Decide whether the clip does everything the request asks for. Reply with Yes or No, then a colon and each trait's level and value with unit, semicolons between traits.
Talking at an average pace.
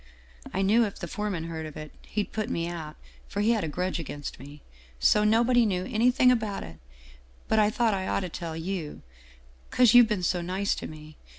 No: fast, 210 wpm